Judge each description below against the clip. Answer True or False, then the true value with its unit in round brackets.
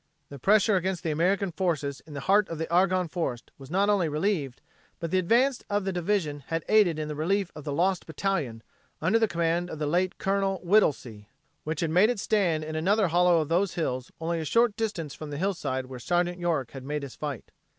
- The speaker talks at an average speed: False (215 wpm)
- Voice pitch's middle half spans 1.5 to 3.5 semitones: False (4.3 semitones)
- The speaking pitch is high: False (170 Hz)